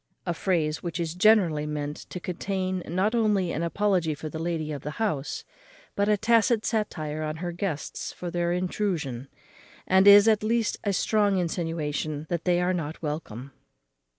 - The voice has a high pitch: No, medium, 175 Hz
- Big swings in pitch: No, average, 4.5 semitones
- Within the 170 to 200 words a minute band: Yes, average, 175 wpm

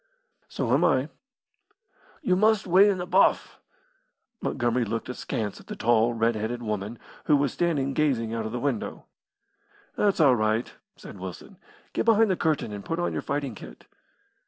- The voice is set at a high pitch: No, low, 125 Hz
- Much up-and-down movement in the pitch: Yes, wide, 7.3 semitones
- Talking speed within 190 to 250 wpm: No, average, 170 wpm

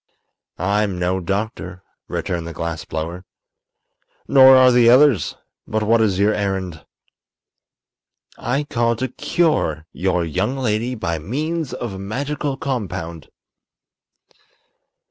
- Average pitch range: No, wide, 6.1 semitones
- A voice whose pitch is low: Yes, low, 105 Hz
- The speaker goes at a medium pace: No, slow, 115 wpm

